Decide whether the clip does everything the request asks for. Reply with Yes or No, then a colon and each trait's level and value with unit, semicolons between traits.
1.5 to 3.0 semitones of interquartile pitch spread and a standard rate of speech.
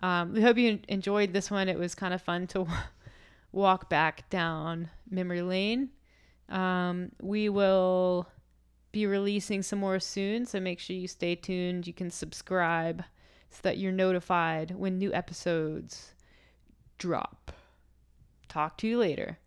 Yes: narrow, 2.4 semitones; average, 150 wpm